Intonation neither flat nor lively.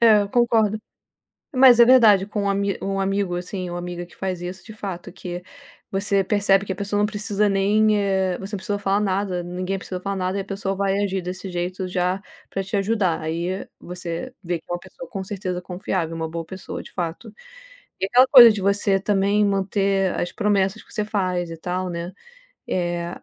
No: narrow, 2.2 semitones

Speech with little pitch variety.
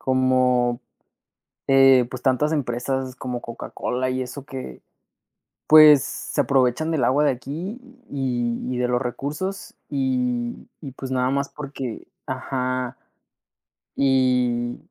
Yes: narrow, 1.9 semitones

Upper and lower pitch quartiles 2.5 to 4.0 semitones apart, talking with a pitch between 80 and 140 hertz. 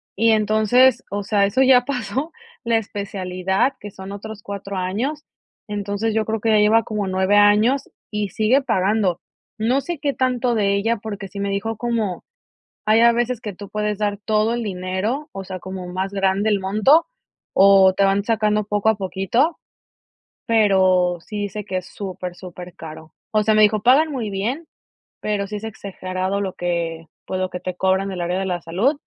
No: average, 2.9 semitones; high, 205 Hz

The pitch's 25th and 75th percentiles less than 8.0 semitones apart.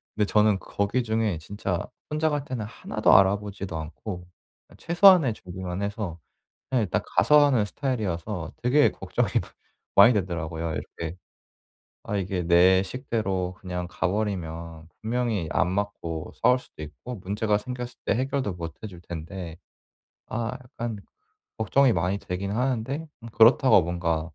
Yes: average, 5.1 semitones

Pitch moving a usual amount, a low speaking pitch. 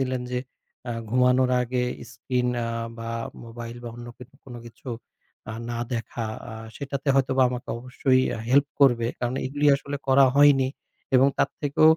No: narrow, 2.1 semitones; low, 130 Hz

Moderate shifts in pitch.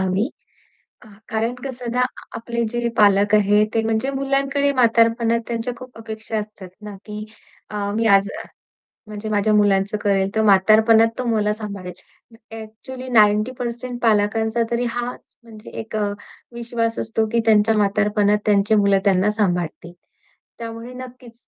No: narrow, 2.2 semitones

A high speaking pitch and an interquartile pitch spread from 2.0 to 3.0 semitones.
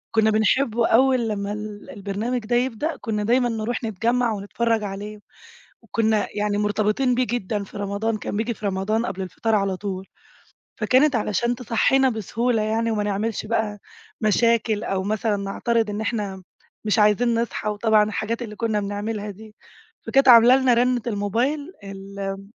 Yes: high, 220 Hz; narrow, 2.4 semitones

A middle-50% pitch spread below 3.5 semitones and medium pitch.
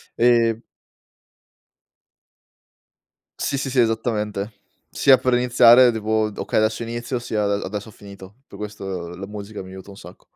No: average, 2.7 semitones; low, 110 Hz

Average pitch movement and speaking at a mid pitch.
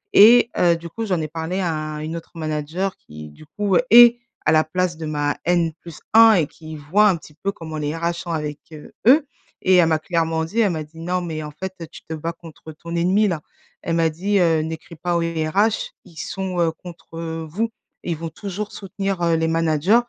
Yes: average, 3.0 semitones; medium, 165 Hz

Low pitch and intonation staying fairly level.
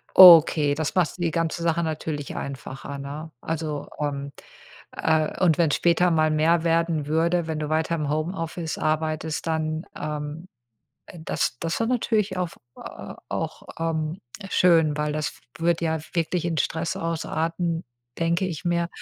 No: medium, 160 Hz; narrow, 1.7 semitones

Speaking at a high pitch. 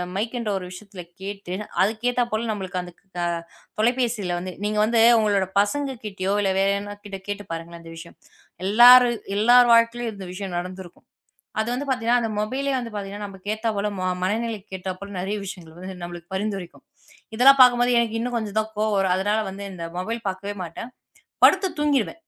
Yes: high, 205 Hz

